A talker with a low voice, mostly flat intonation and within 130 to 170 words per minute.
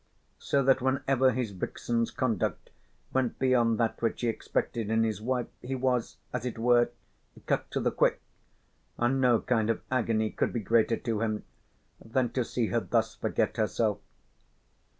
Yes: low, 120 Hz; narrow, 2.2 semitones; average, 165 wpm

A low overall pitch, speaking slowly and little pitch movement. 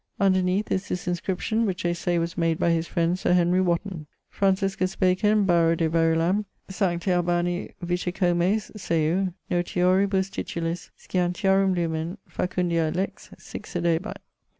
No: medium, 180 Hz; slow, 130 wpm; narrow, 2.0 semitones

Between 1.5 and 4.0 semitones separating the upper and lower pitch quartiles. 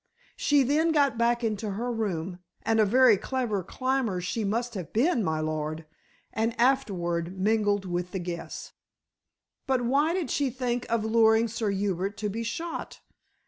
No: average, 4.4 semitones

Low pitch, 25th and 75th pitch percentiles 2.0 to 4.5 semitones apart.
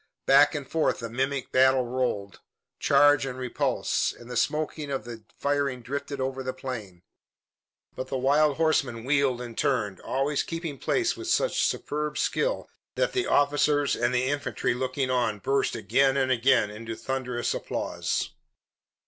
Yes: low, 130 Hz; average, 2.8 semitones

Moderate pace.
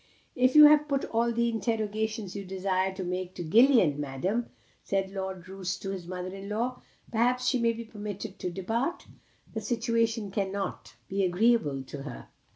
Yes: average, 170 wpm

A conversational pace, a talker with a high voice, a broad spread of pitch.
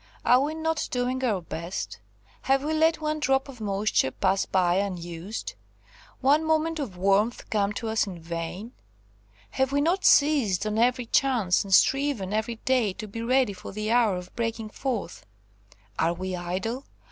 Yes: average, 170 wpm; high, 225 Hz; wide, 5.8 semitones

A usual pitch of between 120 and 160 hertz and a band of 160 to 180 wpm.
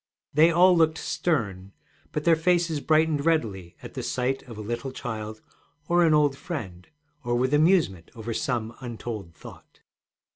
No: low, 135 Hz; average, 150 wpm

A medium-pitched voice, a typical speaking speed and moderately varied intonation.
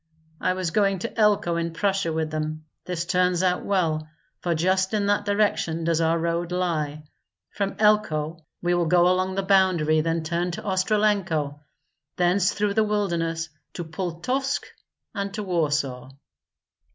Yes: medium, 175 Hz; average, 150 wpm; average, 3.4 semitones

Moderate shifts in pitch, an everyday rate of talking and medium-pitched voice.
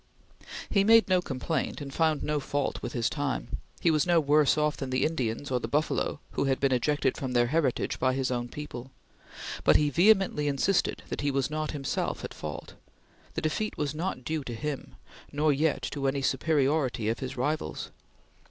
Yes: average, 3.0 semitones; average, 190 wpm; medium, 145 Hz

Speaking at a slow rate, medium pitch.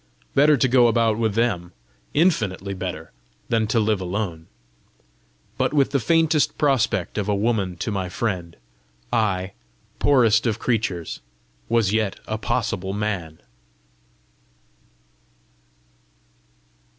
No: slow, 115 wpm; low, 110 Hz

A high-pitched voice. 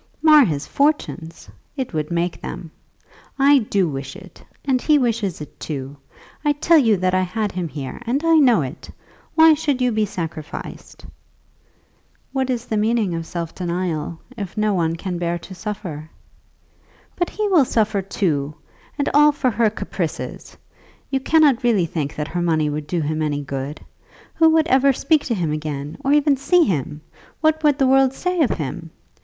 Yes: high, 205 Hz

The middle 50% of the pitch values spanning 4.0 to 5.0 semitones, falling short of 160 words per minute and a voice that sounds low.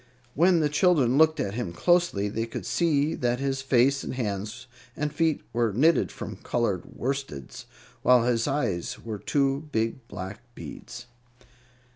Yes: average, 4.7 semitones; average, 150 wpm; low, 125 Hz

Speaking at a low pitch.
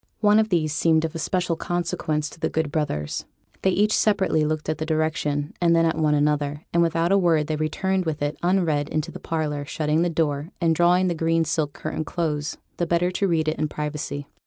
No: medium, 160 Hz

